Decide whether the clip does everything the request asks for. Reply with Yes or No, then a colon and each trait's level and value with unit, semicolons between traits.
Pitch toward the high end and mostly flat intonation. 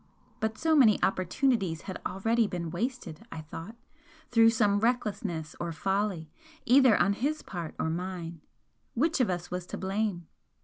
No: high, 200 Hz; average, 4.8 semitones